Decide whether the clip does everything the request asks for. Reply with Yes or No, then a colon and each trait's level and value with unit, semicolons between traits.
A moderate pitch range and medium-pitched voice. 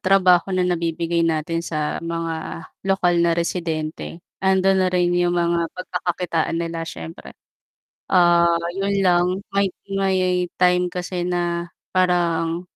No: narrow, 1.5 semitones; medium, 175 Hz